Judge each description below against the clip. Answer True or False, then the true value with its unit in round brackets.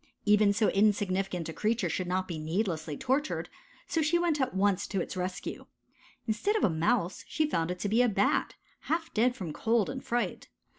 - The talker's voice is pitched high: True (205 Hz)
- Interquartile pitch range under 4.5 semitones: False (5.3 semitones)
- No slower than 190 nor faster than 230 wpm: True (195 wpm)